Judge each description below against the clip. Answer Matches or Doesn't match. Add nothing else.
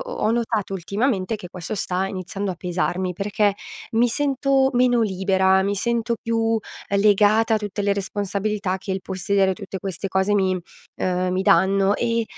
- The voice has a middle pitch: Doesn't match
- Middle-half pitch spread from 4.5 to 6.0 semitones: Doesn't match